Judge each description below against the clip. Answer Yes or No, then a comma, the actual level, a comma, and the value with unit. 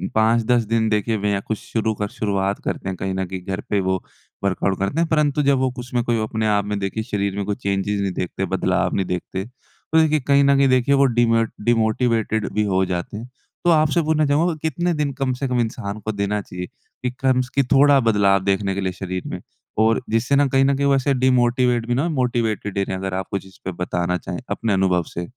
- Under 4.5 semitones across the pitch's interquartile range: No, average, 5.1 semitones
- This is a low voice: Yes, low, 110 Hz